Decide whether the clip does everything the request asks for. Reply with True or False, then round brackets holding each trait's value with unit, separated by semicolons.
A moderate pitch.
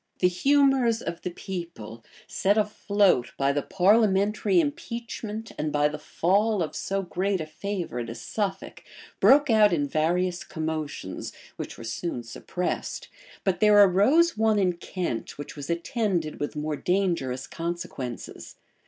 True (180 Hz)